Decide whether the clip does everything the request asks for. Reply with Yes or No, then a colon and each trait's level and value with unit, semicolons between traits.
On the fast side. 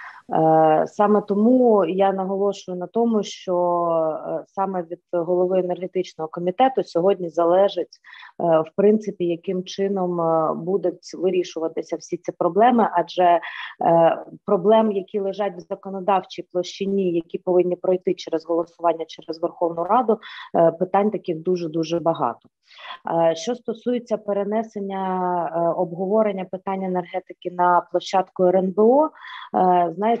No: slow, 105 wpm